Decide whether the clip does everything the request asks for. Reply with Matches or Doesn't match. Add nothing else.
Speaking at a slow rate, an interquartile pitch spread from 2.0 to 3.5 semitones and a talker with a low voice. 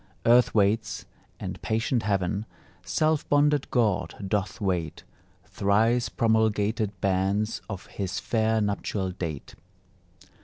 Matches